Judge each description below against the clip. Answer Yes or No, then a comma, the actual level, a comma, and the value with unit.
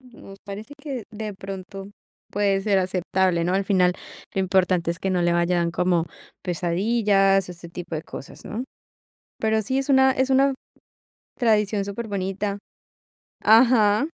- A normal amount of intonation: Yes, average, 3.3 semitones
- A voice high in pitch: Yes, high, 195 Hz